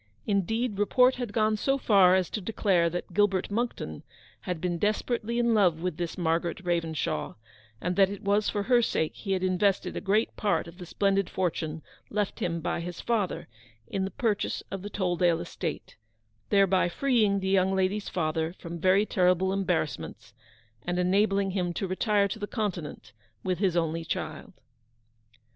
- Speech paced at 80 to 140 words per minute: No, average, 170 wpm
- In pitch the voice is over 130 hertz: Yes, high, 190 Hz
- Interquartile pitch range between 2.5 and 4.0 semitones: Yes, average, 2.9 semitones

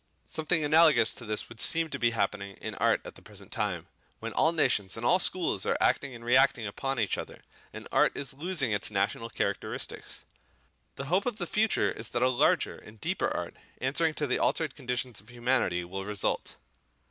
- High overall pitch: No, low, 125 Hz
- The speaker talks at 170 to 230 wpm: Yes, average, 195 wpm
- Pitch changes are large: Yes, wide, 6.0 semitones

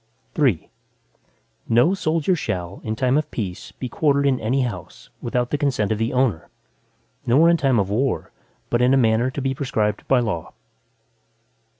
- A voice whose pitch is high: No, low, 125 Hz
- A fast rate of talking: No, average, 170 wpm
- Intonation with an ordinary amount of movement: Yes, average, 4.2 semitones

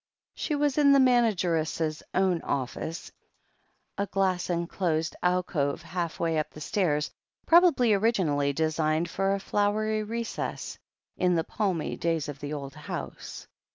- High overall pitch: No, medium, 175 Hz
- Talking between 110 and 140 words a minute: Yes, slow, 135 wpm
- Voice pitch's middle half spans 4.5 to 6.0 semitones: Yes, average, 5.0 semitones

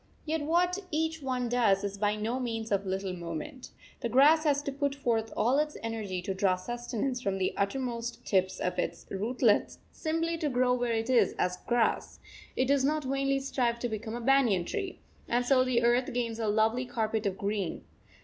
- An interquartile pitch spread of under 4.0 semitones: No, average, 4.5 semitones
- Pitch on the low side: No, high, 240 Hz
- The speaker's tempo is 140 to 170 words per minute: No, average, 195 wpm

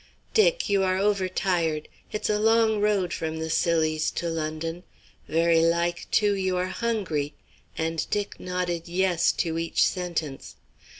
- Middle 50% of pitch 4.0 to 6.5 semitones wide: No, average, 3.4 semitones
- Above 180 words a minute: No, average, 145 wpm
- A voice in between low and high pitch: Yes, medium, 175 Hz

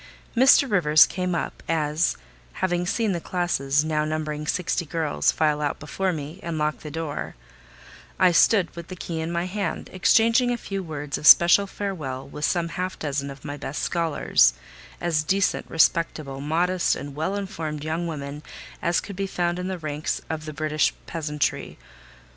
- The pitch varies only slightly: No, average, 3.2 semitones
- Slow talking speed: No, average, 170 wpm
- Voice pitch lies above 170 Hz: No, medium, 165 Hz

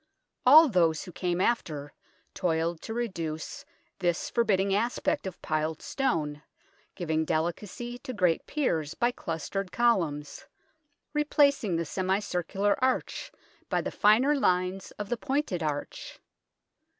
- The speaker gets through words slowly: Yes, slow, 125 wpm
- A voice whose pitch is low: No, medium, 185 Hz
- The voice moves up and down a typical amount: No, wide, 6.5 semitones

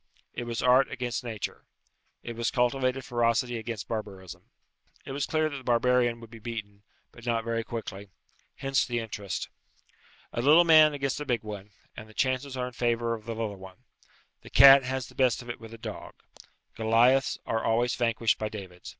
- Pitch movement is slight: Yes, narrow, 2.3 semitones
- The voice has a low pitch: Yes, low, 120 Hz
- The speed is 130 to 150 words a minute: No, average, 190 wpm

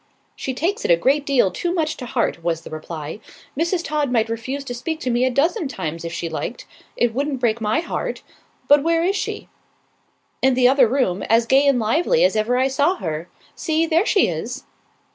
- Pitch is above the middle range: Yes, very high, 260 Hz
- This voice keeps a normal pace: No, fast, 210 wpm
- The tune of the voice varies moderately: No, wide, 5.9 semitones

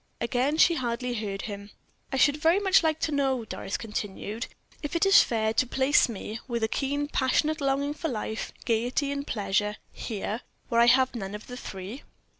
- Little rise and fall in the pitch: No, average, 4.6 semitones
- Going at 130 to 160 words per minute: No, average, 190 wpm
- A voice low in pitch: No, very high, 250 Hz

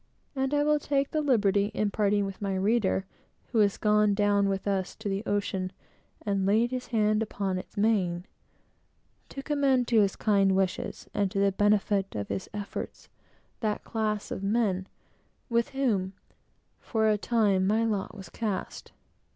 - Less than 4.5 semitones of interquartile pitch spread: Yes, narrow, 2.5 semitones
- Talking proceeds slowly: No, average, 165 wpm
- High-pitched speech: Yes, high, 205 Hz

